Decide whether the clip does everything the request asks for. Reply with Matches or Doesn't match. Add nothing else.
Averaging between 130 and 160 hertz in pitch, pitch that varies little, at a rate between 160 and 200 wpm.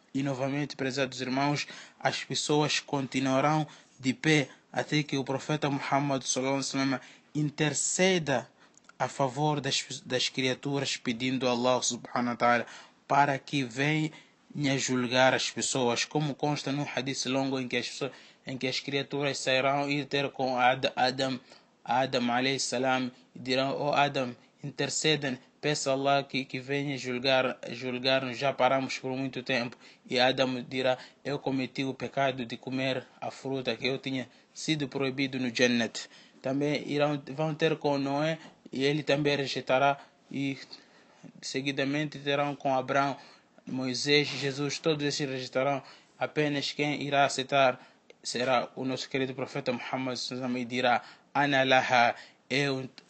Doesn't match